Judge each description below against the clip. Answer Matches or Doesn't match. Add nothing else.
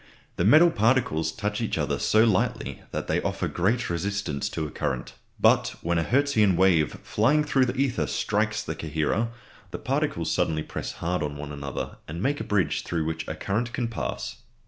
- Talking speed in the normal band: Matches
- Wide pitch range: Matches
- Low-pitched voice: Matches